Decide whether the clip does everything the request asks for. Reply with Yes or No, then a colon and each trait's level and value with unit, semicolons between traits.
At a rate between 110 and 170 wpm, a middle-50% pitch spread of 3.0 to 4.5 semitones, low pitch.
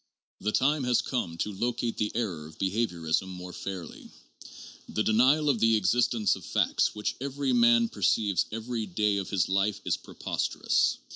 Yes: average, 160 wpm; average, 4.0 semitones; low, 110 Hz